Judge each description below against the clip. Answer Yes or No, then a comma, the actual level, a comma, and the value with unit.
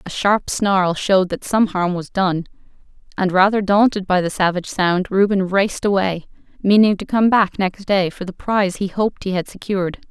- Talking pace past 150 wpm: Yes, average, 195 wpm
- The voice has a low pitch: No, high, 190 Hz